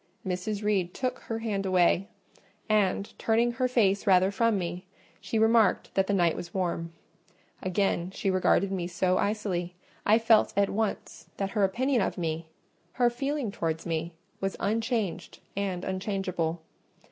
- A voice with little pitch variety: No, average, 3.5 semitones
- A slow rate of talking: No, average, 145 wpm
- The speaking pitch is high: Yes, high, 195 Hz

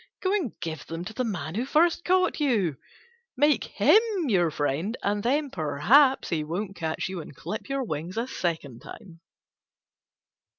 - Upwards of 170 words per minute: No, average, 165 wpm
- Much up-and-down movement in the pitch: Yes, wide, 8.6 semitones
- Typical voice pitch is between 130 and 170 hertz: No, high, 200 Hz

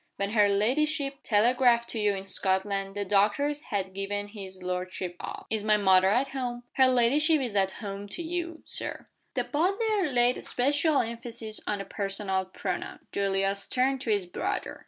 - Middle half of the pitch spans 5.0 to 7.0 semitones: Yes, average, 5.3 semitones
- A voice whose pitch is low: No, high, 215 Hz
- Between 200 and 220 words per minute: No, average, 175 wpm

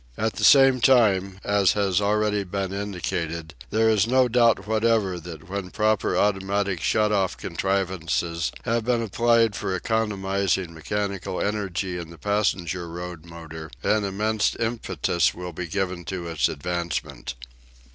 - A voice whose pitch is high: No, very low, 95 Hz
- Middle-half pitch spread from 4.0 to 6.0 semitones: No, average, 3.3 semitones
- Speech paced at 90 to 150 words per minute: Yes, average, 140 wpm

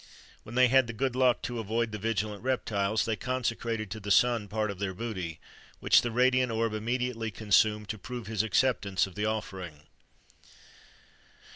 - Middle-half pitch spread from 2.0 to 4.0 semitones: Yes, average, 2.8 semitones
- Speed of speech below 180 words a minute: Yes, average, 170 wpm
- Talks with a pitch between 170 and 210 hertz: No, low, 110 Hz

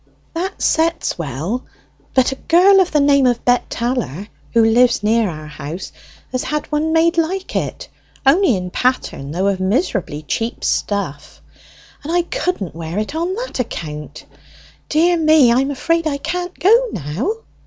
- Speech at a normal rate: Yes, average, 165 wpm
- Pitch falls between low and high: No, very high, 255 Hz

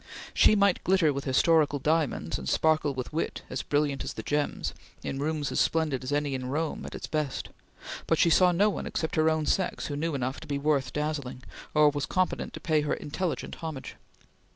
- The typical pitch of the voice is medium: Yes, medium, 150 Hz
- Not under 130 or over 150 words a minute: No, fast, 205 wpm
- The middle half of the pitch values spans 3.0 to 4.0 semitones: No, narrow, 2.4 semitones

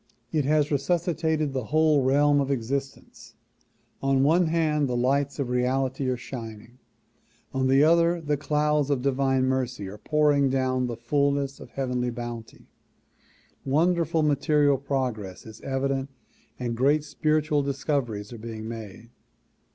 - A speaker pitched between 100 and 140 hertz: Yes, low, 135 Hz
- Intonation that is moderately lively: Yes, average, 3.0 semitones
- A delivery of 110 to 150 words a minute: Yes, slow, 135 wpm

